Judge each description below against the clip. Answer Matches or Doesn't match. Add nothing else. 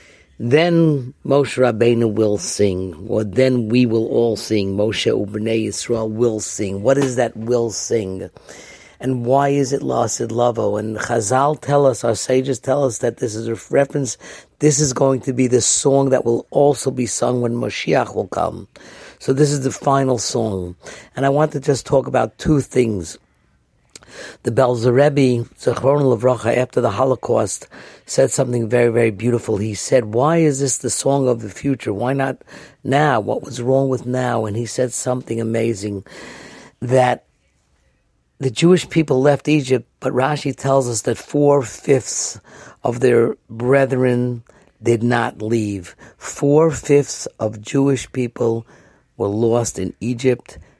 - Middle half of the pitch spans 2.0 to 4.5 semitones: Matches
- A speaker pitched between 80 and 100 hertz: Doesn't match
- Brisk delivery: Doesn't match